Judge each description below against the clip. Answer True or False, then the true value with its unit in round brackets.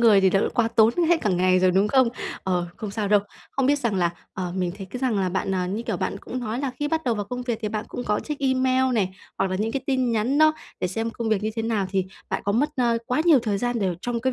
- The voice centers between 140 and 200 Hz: False (225 Hz)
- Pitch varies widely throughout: False (4.6 semitones)